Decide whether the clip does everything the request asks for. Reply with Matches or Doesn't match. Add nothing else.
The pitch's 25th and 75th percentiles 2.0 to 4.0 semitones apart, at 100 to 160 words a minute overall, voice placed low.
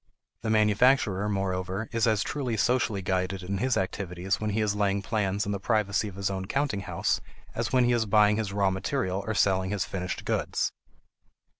Doesn't match